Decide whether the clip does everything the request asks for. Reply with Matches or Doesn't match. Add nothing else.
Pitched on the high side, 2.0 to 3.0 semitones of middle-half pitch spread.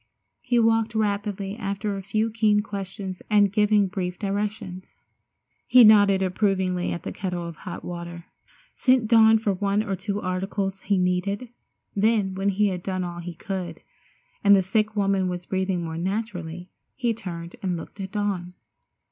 Matches